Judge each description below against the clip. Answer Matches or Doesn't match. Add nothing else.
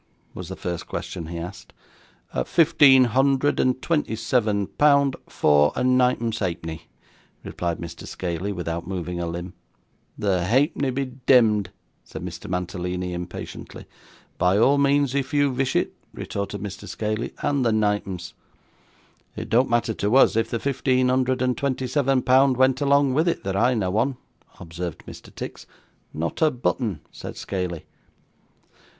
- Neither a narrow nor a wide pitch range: Doesn't match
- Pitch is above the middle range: Doesn't match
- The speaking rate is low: Doesn't match